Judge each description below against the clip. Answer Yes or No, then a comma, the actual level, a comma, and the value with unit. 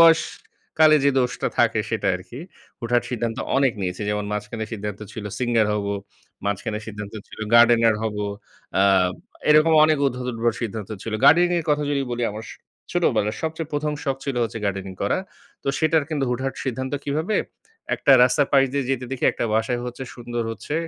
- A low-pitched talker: Yes, low, 120 Hz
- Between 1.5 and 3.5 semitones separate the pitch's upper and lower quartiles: No, average, 4.4 semitones